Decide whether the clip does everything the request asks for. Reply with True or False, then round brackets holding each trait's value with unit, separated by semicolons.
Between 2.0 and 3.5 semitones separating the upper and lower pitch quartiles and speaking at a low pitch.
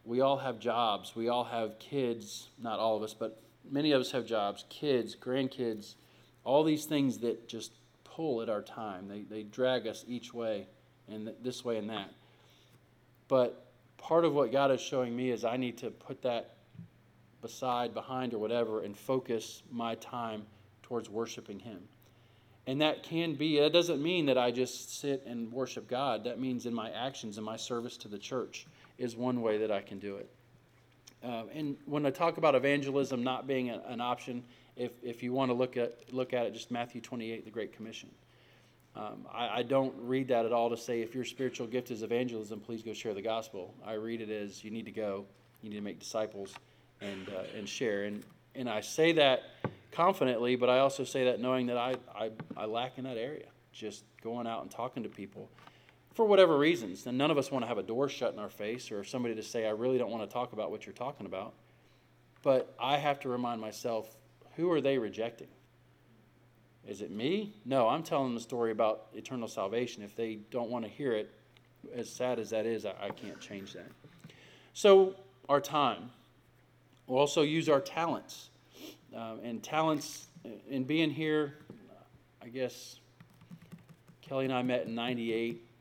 True (2.7 semitones; 120 Hz)